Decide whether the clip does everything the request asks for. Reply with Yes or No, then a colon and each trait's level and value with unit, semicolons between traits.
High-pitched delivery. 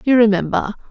Yes: high, 215 Hz